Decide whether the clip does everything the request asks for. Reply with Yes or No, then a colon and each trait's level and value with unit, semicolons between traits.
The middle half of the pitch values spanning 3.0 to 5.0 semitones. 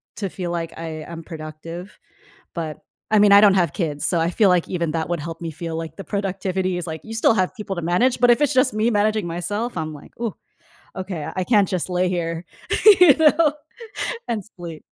Yes: average, 4.0 semitones